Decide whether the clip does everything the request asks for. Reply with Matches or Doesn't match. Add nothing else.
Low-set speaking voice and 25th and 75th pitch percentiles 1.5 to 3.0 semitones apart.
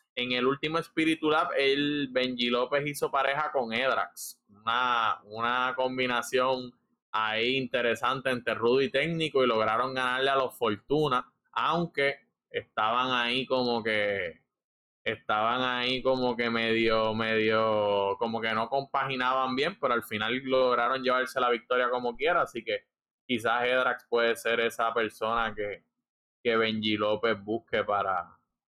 Matches